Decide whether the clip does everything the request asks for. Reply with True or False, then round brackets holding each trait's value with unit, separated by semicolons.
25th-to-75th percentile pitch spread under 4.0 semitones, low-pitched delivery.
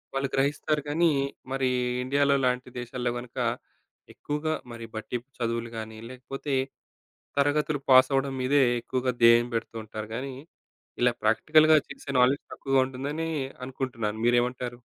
True (2.8 semitones; 130 Hz)